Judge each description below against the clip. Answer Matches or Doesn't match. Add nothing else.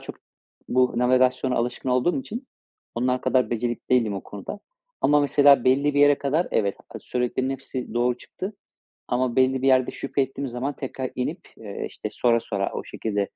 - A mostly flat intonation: Matches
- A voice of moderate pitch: Doesn't match